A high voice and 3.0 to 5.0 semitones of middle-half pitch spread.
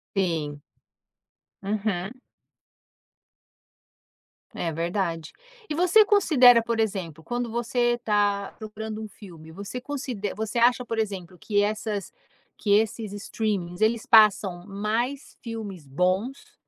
Yes: high, 215 Hz; average, 3.7 semitones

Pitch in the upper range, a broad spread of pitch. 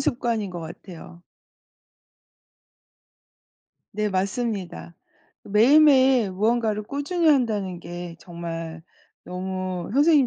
Yes: high, 200 Hz; wide, 5.9 semitones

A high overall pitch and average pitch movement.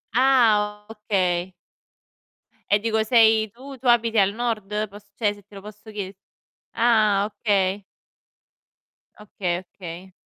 No: high, 210 Hz; narrow, 2.2 semitones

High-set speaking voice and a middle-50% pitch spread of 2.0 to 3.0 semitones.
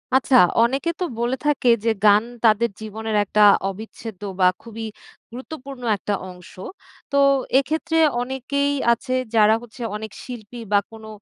No: high, 235 Hz; average, 3.6 semitones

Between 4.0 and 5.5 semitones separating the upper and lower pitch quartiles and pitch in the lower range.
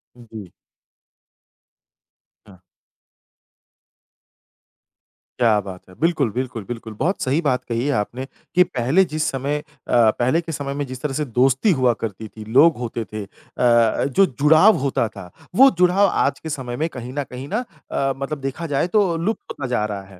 Yes: average, 4.6 semitones; low, 130 Hz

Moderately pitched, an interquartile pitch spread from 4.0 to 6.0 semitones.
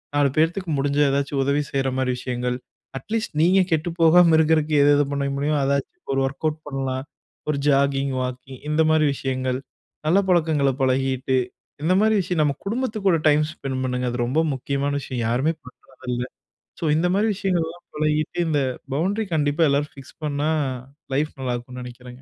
No: medium, 145 Hz; average, 3.4 semitones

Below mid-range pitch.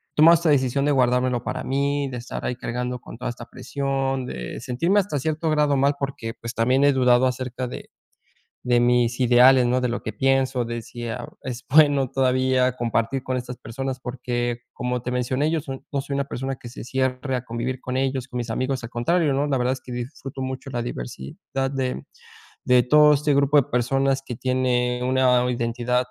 Yes: low, 130 Hz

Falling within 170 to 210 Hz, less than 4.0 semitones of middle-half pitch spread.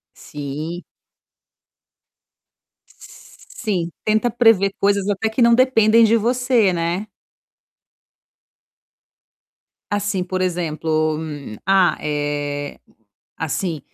No: high, 190 Hz; wide, 5.6 semitones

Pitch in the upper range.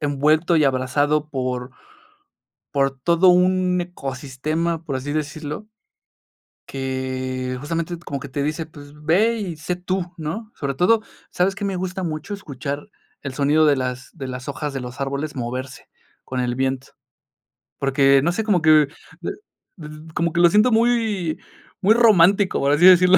No: medium, 155 Hz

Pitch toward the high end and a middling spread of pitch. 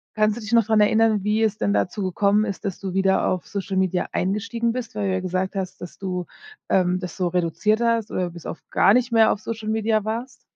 Yes: high, 205 Hz; average, 3.0 semitones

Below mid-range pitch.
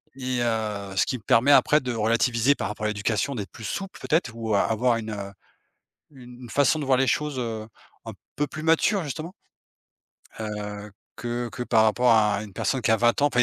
Yes: low, 120 Hz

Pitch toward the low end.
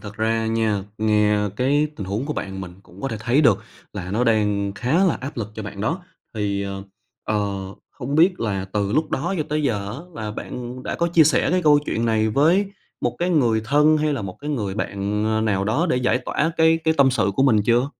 Yes: low, 115 Hz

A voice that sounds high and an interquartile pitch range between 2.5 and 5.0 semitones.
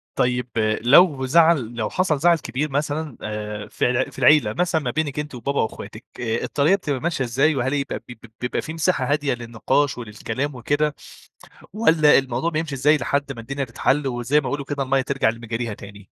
No: low, 135 Hz; average, 3.7 semitones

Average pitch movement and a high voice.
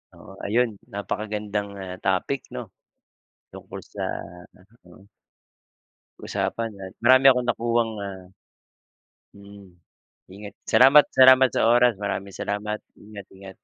No: average, 3.3 semitones; low, 105 Hz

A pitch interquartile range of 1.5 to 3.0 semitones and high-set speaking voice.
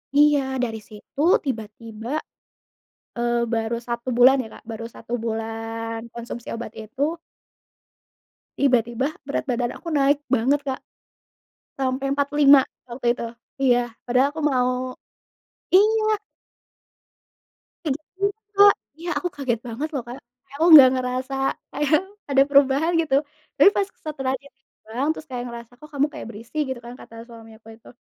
No: average, 3.4 semitones; very high, 255 Hz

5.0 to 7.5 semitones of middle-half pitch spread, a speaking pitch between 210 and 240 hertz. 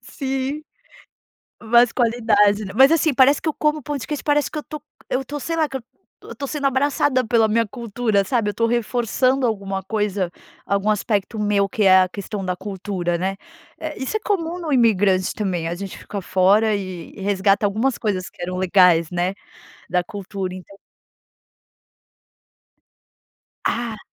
Yes: average, 5.3 semitones; high, 215 Hz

